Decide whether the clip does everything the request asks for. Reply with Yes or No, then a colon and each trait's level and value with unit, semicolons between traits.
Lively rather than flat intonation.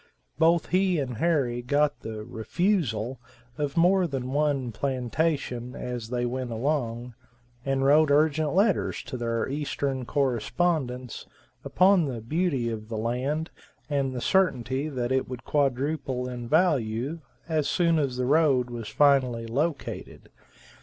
No: average, 4.1 semitones